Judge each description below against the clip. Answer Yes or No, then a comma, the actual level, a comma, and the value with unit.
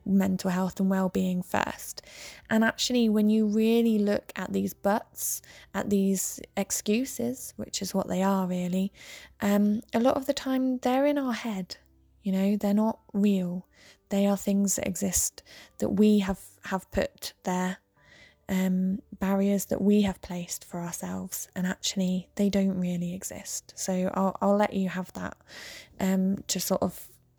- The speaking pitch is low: No, high, 195 Hz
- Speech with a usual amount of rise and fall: No, narrow, 2.2 semitones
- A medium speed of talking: Yes, average, 160 wpm